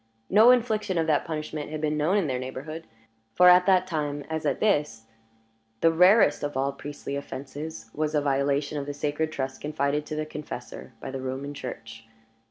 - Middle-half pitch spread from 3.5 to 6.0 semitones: No, narrow, 2.5 semitones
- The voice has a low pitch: No, medium, 150 Hz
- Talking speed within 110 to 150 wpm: No, average, 185 wpm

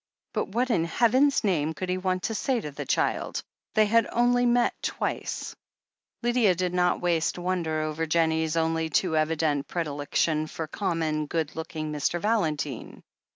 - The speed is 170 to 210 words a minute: No, average, 160 wpm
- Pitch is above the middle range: No, medium, 165 Hz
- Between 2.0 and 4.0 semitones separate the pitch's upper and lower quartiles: No, average, 4.8 semitones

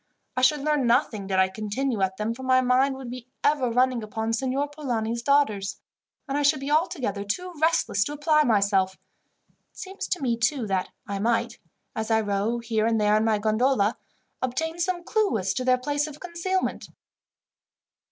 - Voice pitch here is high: Yes, very high, 250 Hz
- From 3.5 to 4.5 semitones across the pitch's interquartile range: No, average, 5.2 semitones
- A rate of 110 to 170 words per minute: No, average, 185 wpm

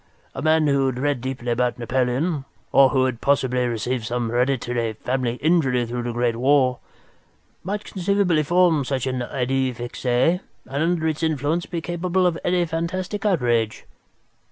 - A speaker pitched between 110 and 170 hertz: Yes, low, 135 Hz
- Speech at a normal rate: Yes, average, 155 wpm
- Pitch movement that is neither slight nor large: Yes, average, 5.0 semitones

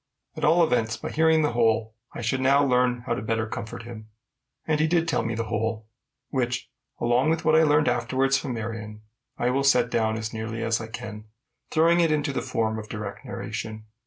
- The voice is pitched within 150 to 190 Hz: No, low, 120 Hz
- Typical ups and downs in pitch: Yes, average, 4.2 semitones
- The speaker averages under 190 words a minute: No, fast, 205 wpm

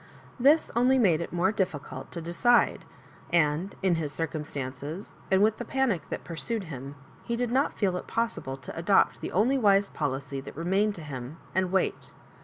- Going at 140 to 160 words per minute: No, average, 195 wpm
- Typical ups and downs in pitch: No, wide, 6.2 semitones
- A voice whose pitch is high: No, medium, 180 Hz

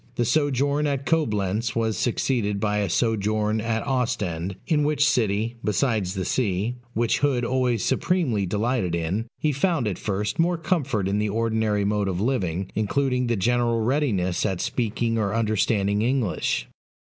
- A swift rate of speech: No, average, 155 wpm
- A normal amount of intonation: Yes, average, 4.0 semitones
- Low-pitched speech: Yes, low, 115 Hz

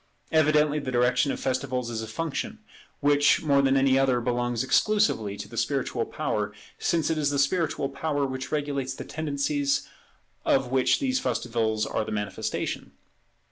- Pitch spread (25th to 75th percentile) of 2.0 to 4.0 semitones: Yes, average, 3.2 semitones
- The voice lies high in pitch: No, low, 135 Hz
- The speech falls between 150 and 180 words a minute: Yes, average, 160 wpm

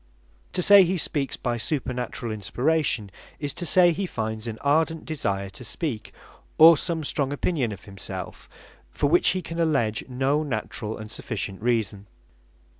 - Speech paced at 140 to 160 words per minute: Yes, average, 155 wpm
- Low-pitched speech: Yes, low, 130 Hz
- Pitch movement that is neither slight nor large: No, wide, 6.8 semitones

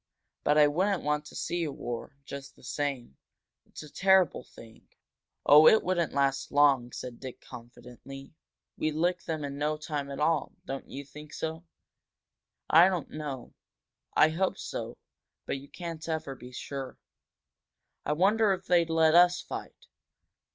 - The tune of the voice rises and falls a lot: No, average, 3.4 semitones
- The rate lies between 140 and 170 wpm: Yes, average, 160 wpm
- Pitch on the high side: No, medium, 150 Hz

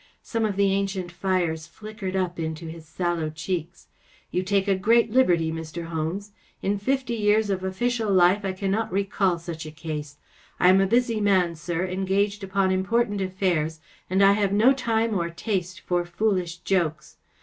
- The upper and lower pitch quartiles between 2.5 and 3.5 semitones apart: Yes, average, 3.1 semitones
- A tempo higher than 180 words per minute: No, average, 175 wpm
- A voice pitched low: No, high, 190 Hz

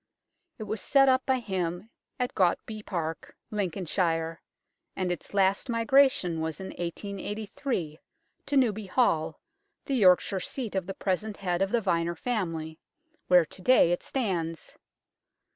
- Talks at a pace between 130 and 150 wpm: Yes, average, 140 wpm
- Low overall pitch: No, high, 190 Hz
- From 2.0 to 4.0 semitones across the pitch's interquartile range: No, average, 4.5 semitones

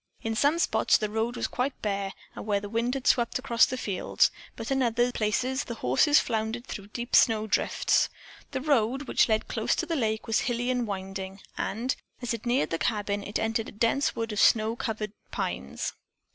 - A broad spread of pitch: No, average, 2.8 semitones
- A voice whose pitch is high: Yes, high, 225 Hz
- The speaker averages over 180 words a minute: Yes, average, 200 wpm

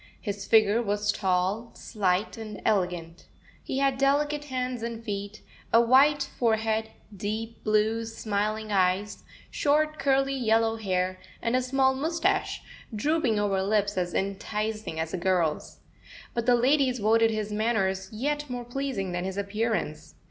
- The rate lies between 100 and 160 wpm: Yes, average, 140 wpm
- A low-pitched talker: No, high, 220 Hz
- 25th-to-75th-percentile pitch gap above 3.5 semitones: Yes, average, 4.0 semitones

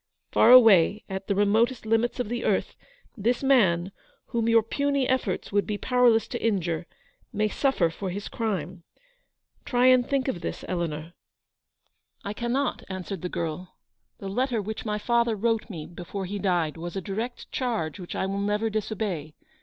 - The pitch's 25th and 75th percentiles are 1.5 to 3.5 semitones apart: No, average, 4.5 semitones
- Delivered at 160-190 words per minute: Yes, average, 170 wpm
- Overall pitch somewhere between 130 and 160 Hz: No, high, 210 Hz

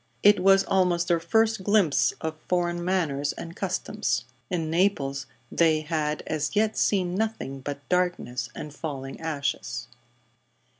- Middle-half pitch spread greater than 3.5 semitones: Yes, average, 4.6 semitones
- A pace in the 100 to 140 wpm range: Yes, slow, 135 wpm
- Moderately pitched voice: Yes, medium, 170 Hz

